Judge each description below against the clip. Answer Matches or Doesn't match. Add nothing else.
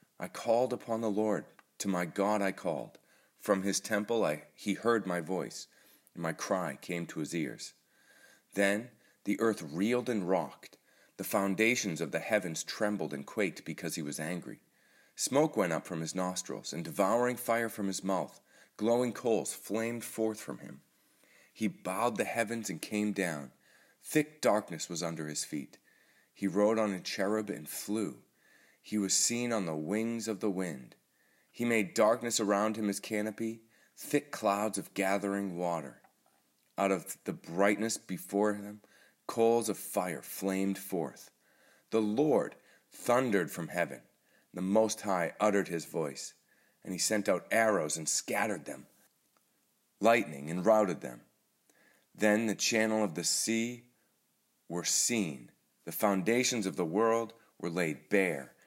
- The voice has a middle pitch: Doesn't match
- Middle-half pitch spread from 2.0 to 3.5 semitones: Matches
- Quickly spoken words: Doesn't match